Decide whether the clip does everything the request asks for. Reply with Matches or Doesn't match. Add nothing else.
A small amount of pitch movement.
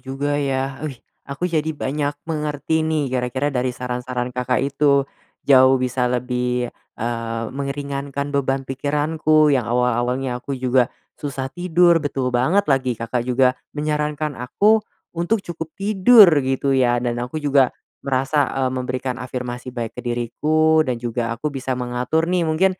Doesn't match